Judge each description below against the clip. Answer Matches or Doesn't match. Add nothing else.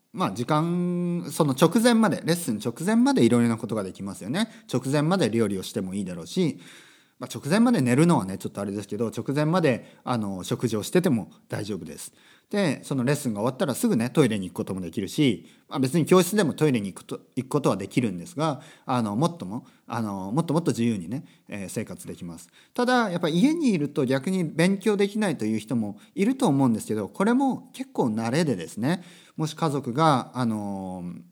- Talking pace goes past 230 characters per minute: Matches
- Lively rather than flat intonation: Matches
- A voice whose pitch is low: Doesn't match